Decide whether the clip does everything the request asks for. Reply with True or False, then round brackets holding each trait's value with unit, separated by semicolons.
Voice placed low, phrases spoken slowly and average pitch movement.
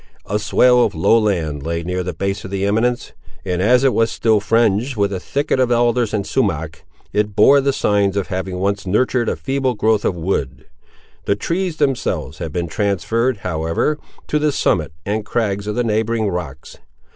False (105 Hz; 190 wpm; 4.6 semitones)